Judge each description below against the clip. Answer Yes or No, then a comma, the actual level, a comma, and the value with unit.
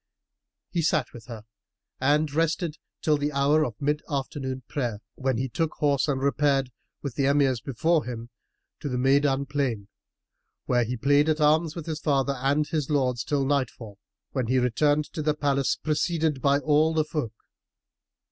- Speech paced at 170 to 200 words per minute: Yes, average, 175 wpm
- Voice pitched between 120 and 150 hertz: Yes, medium, 140 Hz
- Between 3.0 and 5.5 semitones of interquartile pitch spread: No, narrow, 2.6 semitones